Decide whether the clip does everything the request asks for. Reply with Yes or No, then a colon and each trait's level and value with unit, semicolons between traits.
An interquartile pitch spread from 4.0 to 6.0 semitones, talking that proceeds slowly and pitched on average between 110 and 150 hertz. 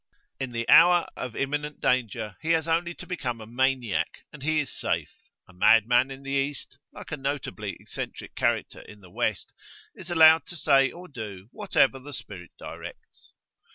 No: average, 4.6 semitones; average, 175 wpm; low, 135 Hz